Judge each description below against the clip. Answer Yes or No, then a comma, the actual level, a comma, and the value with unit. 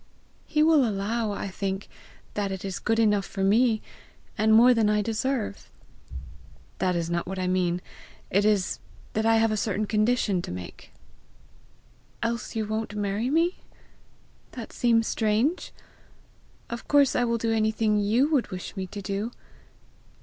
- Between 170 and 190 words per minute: No, average, 155 wpm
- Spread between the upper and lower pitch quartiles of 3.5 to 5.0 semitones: No, average, 2.8 semitones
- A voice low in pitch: No, high, 215 Hz